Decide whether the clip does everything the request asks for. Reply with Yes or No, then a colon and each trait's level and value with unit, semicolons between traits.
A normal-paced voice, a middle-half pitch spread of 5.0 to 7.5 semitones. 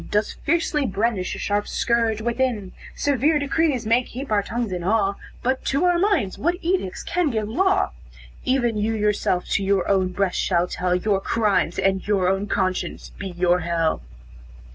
Yes: average, 170 wpm; average, 5.3 semitones